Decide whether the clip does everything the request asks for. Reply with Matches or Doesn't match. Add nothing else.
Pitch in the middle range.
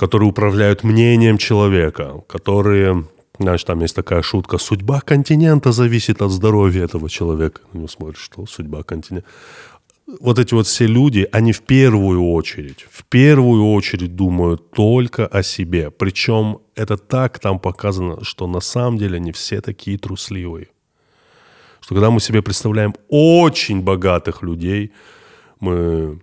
Doesn't match